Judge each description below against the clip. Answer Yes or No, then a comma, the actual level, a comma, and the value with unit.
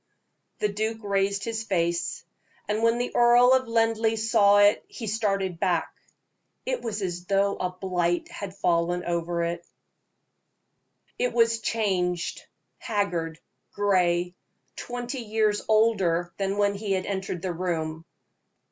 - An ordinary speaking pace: No, slow, 130 wpm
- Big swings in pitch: No, average, 4.0 semitones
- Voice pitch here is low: No, high, 200 Hz